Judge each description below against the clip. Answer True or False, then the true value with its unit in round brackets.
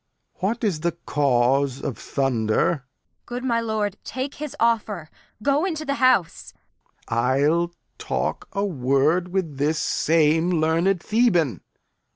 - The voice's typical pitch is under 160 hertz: False (170 Hz)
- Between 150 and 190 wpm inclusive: False (135 wpm)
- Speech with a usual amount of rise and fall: False (7.3 semitones)